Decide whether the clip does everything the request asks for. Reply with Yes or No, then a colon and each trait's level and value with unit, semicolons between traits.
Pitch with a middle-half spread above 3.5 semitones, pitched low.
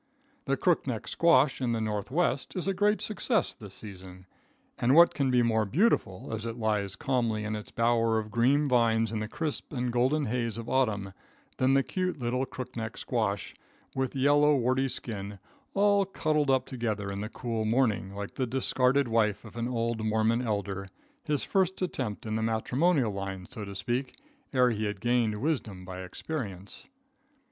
Yes: average, 3.9 semitones; low, 120 Hz